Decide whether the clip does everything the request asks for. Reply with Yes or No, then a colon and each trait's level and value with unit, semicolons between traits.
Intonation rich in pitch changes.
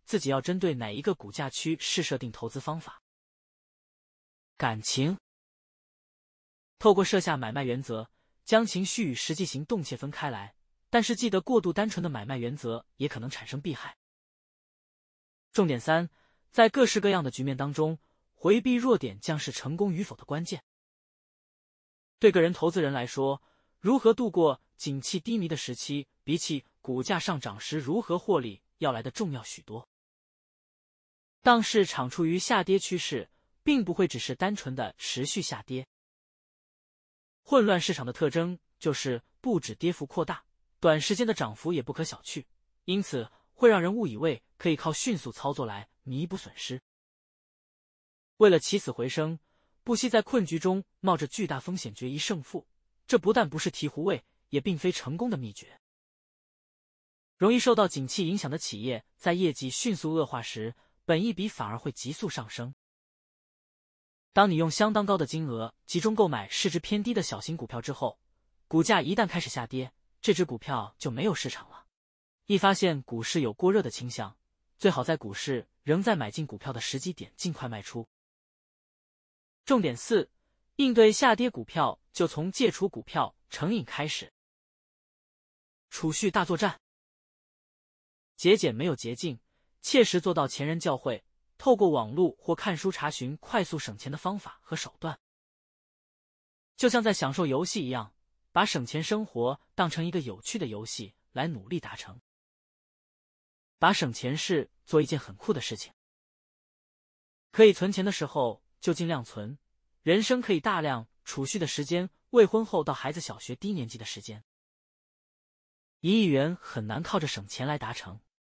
Yes: wide, 7.0 semitones